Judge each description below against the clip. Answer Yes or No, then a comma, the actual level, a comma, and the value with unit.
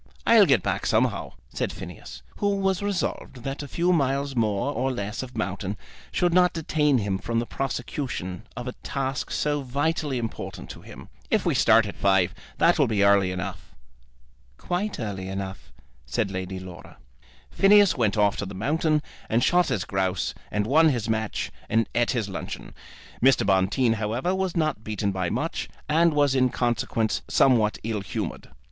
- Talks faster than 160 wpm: Yes, average, 170 wpm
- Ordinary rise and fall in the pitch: No, wide, 6.5 semitones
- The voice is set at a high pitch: No, low, 120 Hz